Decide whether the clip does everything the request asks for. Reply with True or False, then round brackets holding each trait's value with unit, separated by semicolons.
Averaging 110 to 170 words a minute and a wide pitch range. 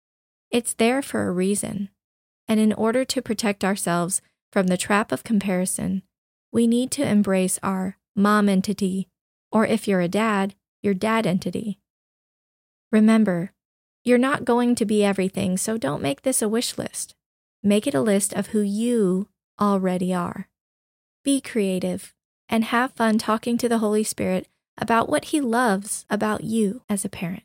False (160 wpm; 3.0 semitones)